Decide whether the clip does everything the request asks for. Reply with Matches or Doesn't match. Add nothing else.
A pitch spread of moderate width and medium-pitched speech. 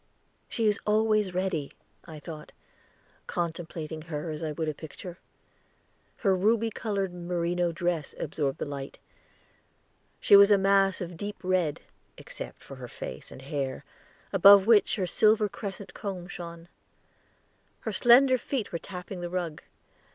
Matches